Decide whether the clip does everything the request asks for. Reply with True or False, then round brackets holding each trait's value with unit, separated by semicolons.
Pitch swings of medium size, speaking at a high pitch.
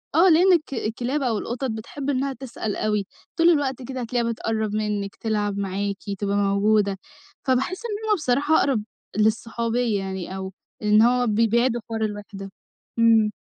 True (4.0 semitones; 225 Hz)